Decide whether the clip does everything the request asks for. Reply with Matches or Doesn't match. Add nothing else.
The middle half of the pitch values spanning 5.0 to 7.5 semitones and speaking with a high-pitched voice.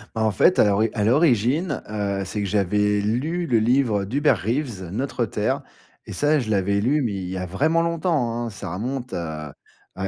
Doesn't match